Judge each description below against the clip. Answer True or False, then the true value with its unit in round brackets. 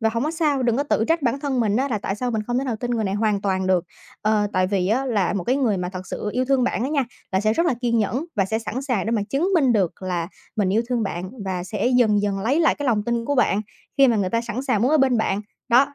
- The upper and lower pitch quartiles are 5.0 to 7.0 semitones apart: False (4.3 semitones)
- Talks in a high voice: True (230 Hz)